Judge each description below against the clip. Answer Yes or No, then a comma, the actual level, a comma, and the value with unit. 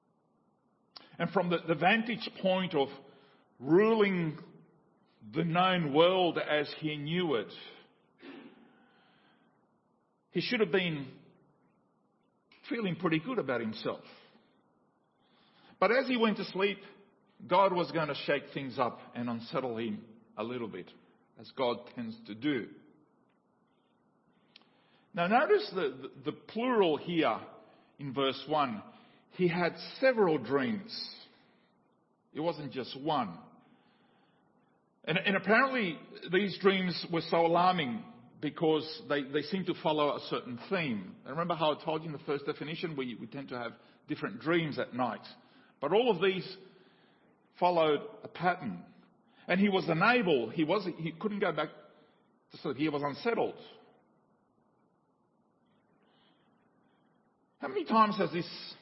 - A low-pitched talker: No, medium, 180 Hz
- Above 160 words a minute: No, slow, 135 wpm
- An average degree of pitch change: No, wide, 6.4 semitones